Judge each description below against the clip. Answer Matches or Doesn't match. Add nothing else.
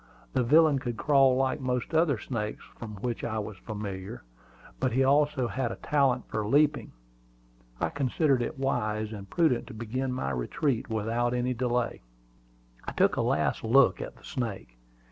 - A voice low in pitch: Matches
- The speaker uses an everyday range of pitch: Matches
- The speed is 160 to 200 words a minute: Matches